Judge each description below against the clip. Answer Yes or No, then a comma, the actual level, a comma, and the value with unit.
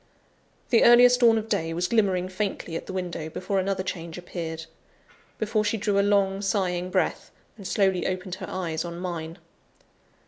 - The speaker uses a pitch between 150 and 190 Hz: Yes, medium, 185 Hz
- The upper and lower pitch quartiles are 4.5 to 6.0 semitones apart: No, narrow, 2.6 semitones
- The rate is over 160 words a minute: Yes, average, 170 wpm